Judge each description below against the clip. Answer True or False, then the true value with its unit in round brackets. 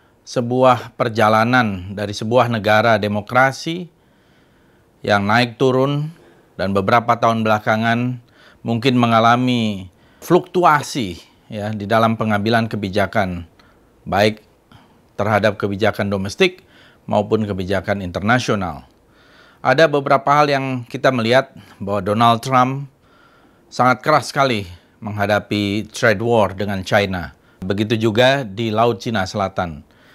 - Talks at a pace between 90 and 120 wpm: True (100 wpm)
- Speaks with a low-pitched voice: True (115 Hz)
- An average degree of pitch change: True (3.6 semitones)